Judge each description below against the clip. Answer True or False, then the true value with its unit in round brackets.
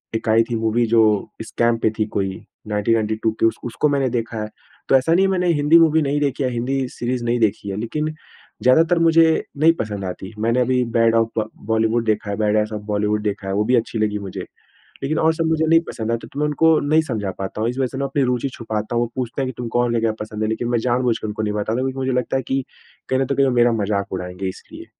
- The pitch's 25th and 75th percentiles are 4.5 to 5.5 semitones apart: False (3.7 semitones)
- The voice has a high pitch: False (115 Hz)